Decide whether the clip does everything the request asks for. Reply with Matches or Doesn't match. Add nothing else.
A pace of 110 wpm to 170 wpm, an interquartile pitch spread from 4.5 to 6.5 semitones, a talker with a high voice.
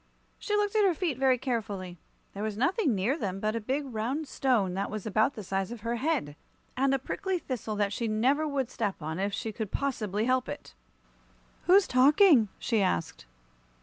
Doesn't match